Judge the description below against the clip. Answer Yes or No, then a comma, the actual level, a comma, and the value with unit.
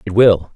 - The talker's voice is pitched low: Yes, low, 100 Hz